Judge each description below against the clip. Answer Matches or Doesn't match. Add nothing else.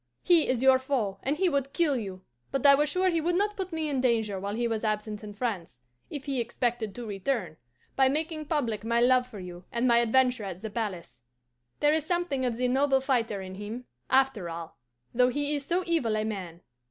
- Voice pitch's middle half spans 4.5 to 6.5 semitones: Matches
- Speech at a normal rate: Doesn't match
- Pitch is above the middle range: Matches